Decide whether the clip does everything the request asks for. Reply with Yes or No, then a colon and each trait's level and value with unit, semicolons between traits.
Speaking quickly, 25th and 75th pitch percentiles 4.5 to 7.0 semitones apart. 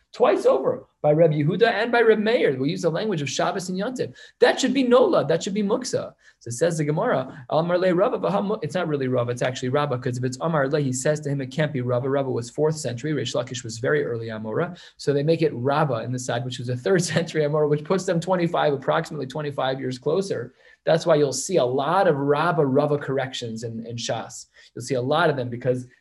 Yes: fast, 235 wpm; average, 5.0 semitones